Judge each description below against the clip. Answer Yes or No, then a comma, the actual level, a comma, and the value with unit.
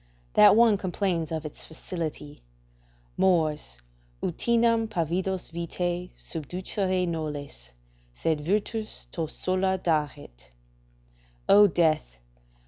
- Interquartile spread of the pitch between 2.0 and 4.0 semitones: Yes, average, 3.5 semitones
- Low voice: No, medium, 170 Hz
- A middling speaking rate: No, slow, 90 wpm